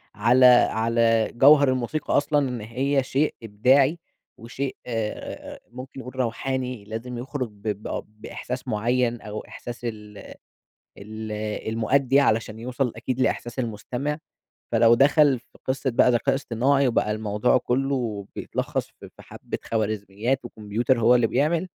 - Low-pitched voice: Yes, low, 120 Hz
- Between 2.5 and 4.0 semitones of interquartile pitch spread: Yes, average, 3.2 semitones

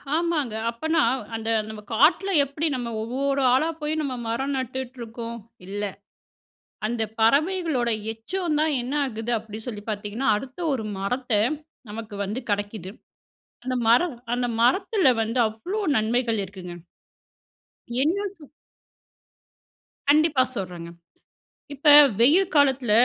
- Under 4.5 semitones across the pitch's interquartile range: No, average, 5.0 semitones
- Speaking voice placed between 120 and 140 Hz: No, very high, 250 Hz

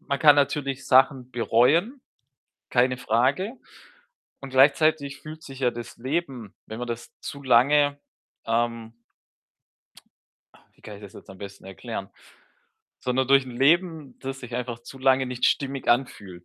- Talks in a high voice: No, low, 130 Hz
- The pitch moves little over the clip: No, average, 3.0 semitones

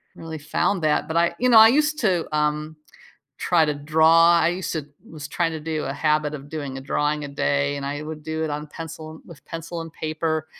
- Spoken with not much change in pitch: Yes, narrow, 1.7 semitones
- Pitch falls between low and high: Yes, medium, 155 Hz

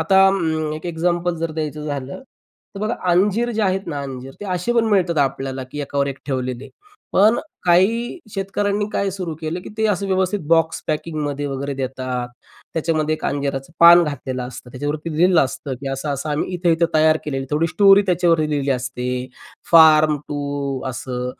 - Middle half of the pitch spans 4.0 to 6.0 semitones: Yes, average, 4.4 semitones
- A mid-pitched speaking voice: Yes, medium, 155 Hz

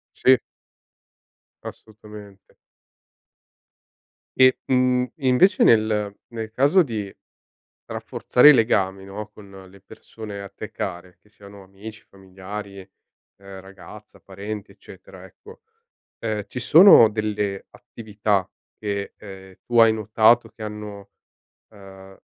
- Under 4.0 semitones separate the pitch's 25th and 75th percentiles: Yes, narrow, 2.5 semitones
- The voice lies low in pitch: Yes, low, 105 Hz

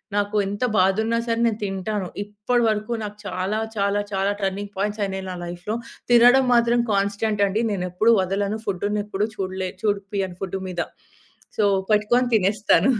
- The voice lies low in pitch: No, high, 205 Hz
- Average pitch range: No, narrow, 1.9 semitones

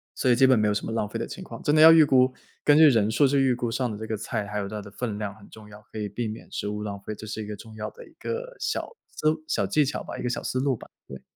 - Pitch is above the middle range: No, low, 115 Hz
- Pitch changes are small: No, average, 4.4 semitones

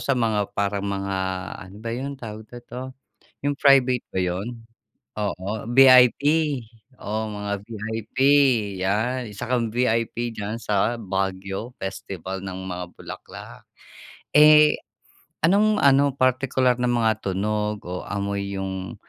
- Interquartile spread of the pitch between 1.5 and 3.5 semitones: No, average, 4.1 semitones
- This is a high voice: No, low, 110 Hz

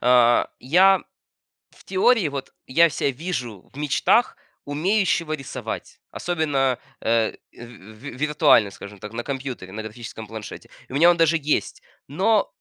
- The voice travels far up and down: Yes, wide, 6.0 semitones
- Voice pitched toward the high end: No, medium, 140 Hz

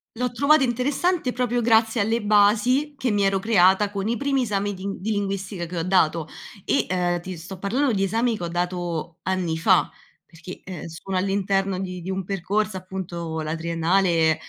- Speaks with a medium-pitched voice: No, high, 195 Hz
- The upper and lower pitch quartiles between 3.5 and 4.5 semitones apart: Yes, average, 4.0 semitones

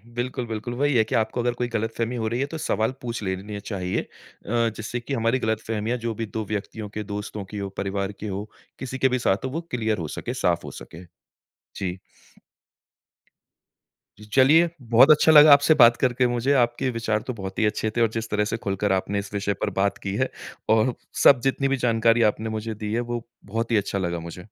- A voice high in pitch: No, low, 115 Hz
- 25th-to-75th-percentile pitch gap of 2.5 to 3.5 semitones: Yes, average, 2.9 semitones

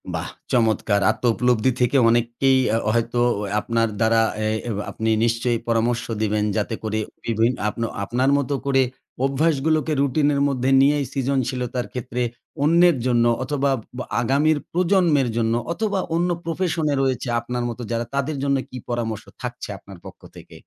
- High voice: No, low, 125 Hz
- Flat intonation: No, average, 3.5 semitones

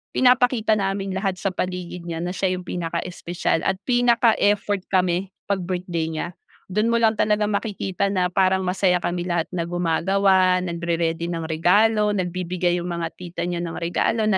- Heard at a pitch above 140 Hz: Yes, medium, 185 Hz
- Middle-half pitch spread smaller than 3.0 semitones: Yes, narrow, 2.5 semitones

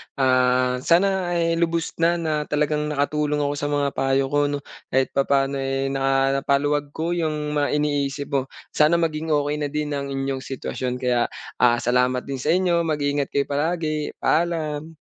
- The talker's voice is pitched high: No, medium, 145 Hz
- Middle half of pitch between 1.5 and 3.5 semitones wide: Yes, narrow, 2.4 semitones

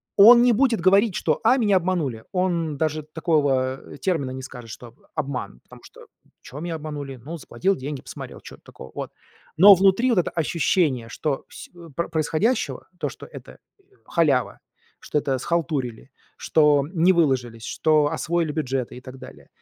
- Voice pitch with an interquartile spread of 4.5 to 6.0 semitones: Yes, average, 5.1 semitones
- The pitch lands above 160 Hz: No, medium, 155 Hz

